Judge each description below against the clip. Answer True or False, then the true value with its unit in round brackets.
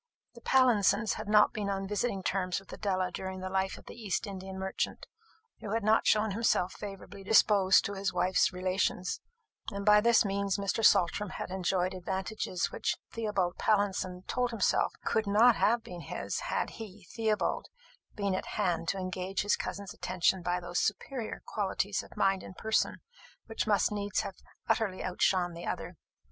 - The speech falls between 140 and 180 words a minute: True (170 wpm)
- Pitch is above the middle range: True (195 Hz)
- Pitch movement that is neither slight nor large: False (2.3 semitones)